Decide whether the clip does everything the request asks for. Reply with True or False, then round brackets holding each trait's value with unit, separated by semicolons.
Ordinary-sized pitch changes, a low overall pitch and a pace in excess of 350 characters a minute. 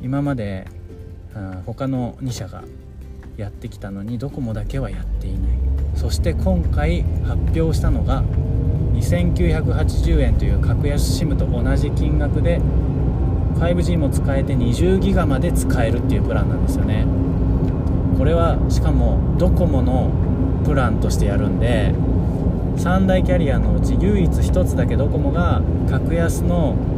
False (4.2 semitones; 90 Hz; 260 characters per minute)